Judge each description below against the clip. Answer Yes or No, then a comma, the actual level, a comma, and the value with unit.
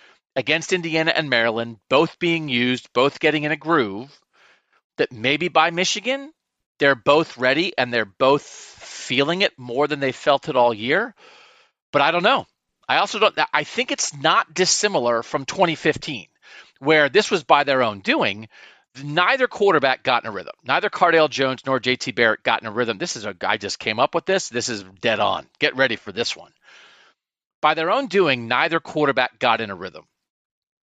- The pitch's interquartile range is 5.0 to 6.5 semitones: Yes, wide, 5.5 semitones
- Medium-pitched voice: Yes, medium, 150 Hz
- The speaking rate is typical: Yes, average, 185 wpm